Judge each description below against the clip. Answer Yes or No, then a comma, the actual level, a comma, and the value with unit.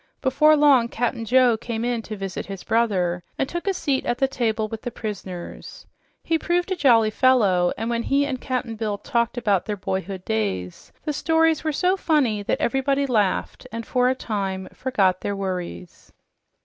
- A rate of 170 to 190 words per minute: Yes, average, 185 wpm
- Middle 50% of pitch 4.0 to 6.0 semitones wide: Yes, average, 5.2 semitones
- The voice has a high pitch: Yes, high, 235 Hz